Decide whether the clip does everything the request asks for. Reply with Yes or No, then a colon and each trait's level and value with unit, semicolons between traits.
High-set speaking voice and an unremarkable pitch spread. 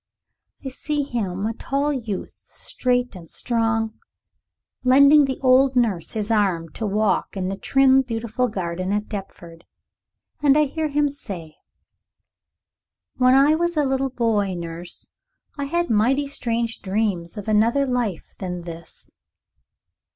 No: high, 230 Hz; wide, 5.7 semitones